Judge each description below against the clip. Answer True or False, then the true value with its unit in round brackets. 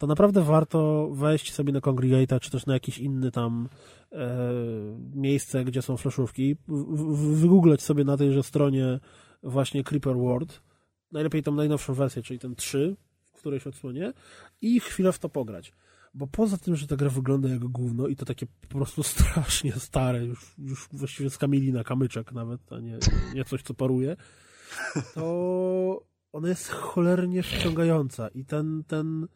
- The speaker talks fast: True (165 wpm)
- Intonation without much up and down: False (3.2 semitones)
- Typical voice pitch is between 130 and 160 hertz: True (140 Hz)